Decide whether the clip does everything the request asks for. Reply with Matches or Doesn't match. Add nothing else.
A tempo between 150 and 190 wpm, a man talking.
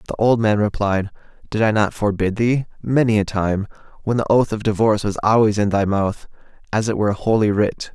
Doesn't match